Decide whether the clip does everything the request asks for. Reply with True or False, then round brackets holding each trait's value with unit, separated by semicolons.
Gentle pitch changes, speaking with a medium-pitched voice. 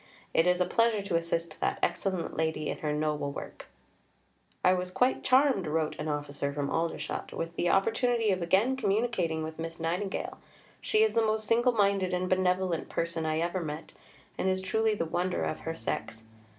False (4.3 semitones; 180 Hz)